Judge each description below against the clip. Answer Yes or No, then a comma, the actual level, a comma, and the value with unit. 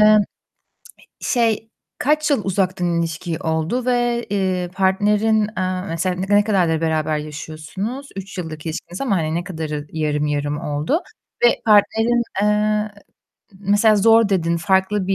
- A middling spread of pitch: Yes, average, 4.7 semitones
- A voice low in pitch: No, high, 190 Hz